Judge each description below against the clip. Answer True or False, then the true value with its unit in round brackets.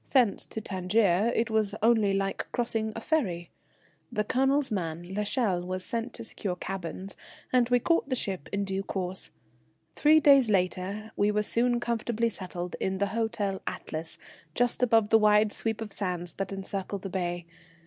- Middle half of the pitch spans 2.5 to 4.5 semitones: True (3.6 semitones)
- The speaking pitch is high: True (205 Hz)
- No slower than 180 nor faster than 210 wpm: False (165 wpm)